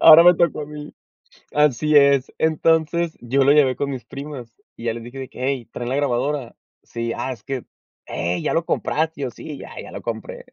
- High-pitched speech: No, medium, 140 Hz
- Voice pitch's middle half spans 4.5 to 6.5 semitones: No, average, 3.5 semitones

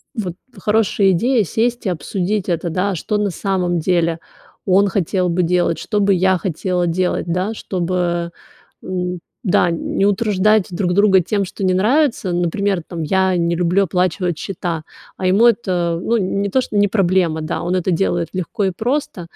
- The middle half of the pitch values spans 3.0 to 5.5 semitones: No, narrow, 2.5 semitones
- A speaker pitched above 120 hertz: Yes, medium, 185 Hz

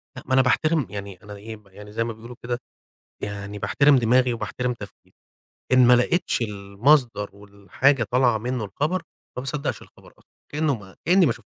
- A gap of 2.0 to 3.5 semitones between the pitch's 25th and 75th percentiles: No, average, 4.3 semitones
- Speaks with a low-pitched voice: Yes, low, 120 Hz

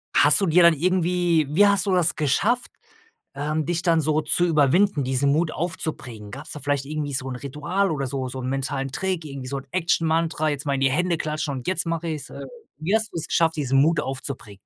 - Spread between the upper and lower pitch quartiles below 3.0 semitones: No, average, 3.7 semitones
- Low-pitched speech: No, medium, 155 Hz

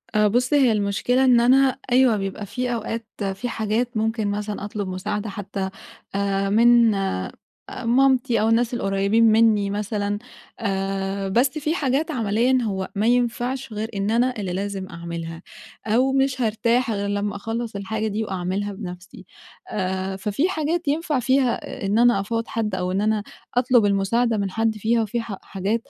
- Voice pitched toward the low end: No, high, 215 Hz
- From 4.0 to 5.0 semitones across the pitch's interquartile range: No, average, 3.4 semitones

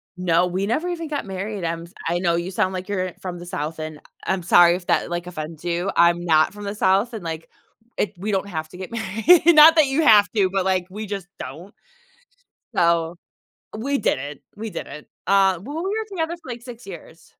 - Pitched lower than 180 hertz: No, high, 190 Hz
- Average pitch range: Yes, average, 4.2 semitones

